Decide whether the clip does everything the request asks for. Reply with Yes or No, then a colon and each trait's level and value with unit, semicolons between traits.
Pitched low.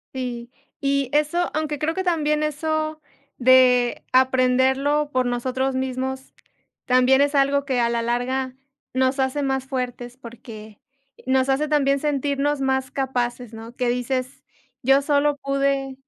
No: very high, 265 Hz